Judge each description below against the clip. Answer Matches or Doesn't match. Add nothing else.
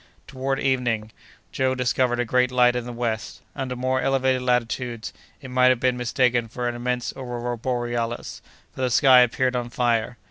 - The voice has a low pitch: Matches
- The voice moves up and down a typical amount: Doesn't match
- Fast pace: Doesn't match